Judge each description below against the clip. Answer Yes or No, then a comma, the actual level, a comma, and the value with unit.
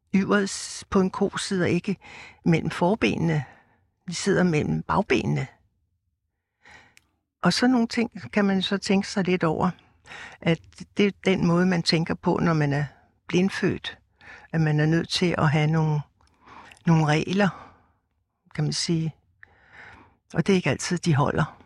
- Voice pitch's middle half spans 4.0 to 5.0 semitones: Yes, average, 4.4 semitones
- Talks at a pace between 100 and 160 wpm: Yes, average, 150 wpm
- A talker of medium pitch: Yes, medium, 170 Hz